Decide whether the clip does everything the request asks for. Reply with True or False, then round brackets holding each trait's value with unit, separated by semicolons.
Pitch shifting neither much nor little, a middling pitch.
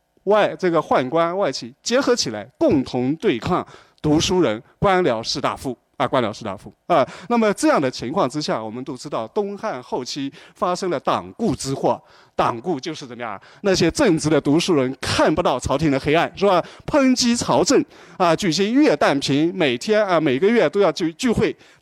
False (7.3 semitones; 170 Hz)